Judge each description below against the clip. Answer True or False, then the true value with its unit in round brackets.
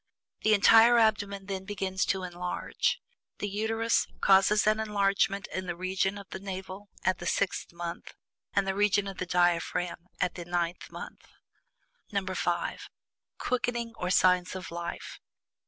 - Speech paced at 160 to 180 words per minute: False (145 wpm)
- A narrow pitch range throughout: True (2.3 semitones)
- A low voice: False (190 Hz)